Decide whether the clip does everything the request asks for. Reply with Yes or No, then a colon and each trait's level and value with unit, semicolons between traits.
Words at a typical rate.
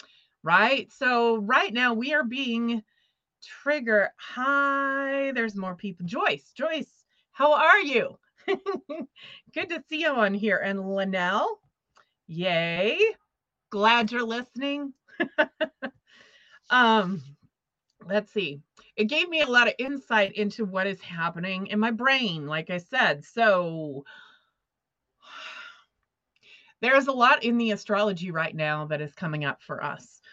No: slow, 125 wpm